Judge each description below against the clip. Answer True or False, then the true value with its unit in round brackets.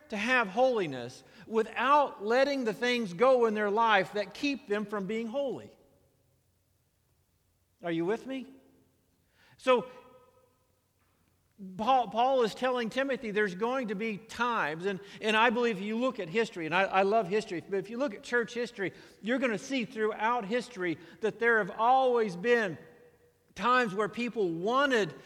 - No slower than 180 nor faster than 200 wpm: False (160 wpm)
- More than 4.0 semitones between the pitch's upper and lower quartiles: True (5.0 semitones)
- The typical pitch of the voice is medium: False (220 Hz)